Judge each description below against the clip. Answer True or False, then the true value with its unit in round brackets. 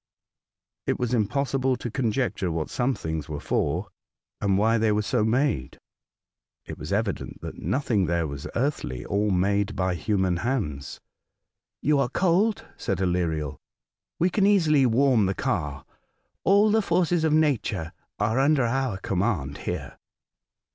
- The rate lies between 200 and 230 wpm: False (145 wpm)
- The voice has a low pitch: True (110 Hz)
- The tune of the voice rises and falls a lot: True (7.2 semitones)